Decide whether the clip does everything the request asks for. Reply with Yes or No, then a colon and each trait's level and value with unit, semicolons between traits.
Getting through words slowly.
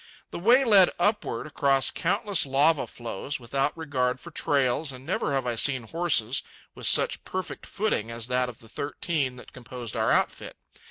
No: average, 170 wpm